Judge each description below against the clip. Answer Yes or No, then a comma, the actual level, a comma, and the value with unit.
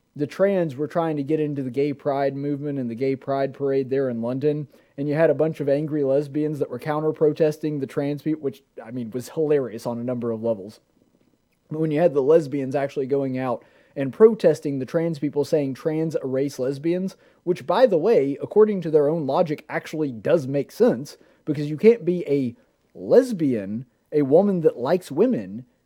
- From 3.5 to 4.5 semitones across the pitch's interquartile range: No, narrow, 2.6 semitones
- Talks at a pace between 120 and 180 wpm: No, average, 200 wpm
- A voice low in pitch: No, medium, 145 Hz